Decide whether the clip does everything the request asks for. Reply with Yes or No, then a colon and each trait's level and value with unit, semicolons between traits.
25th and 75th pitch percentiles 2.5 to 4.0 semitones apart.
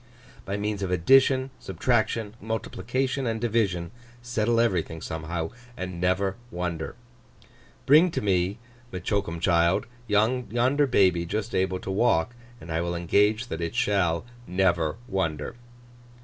No: average, 5.1 semitones